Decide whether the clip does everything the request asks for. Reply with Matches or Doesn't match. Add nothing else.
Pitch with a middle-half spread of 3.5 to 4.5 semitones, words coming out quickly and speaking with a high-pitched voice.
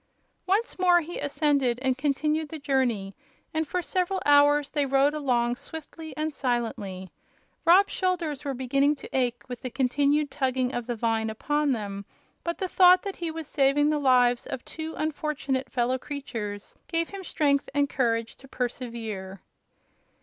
Doesn't match